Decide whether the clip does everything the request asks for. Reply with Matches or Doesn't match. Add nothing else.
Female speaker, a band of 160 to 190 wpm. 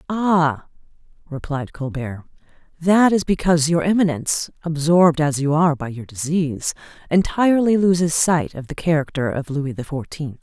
Doesn't match